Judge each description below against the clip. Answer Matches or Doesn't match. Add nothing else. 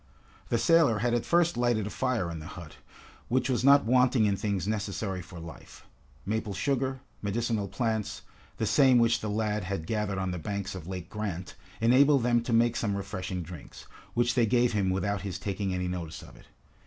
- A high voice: Doesn't match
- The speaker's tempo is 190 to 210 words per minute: Matches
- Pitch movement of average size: Matches